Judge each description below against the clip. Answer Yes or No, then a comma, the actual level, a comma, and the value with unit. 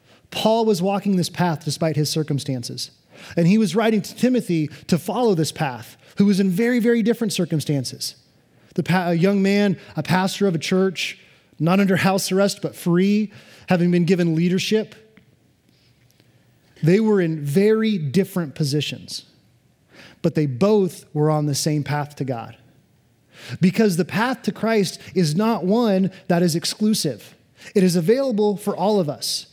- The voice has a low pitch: No, medium, 185 Hz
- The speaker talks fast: No, average, 160 wpm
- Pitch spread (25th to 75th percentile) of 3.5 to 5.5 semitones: Yes, average, 4.9 semitones